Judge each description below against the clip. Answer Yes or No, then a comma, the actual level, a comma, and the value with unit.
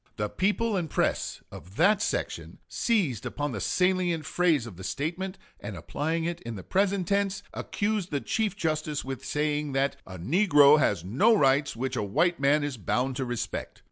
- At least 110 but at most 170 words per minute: No, average, 180 wpm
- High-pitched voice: No, medium, 150 Hz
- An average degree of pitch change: No, wide, 5.9 semitones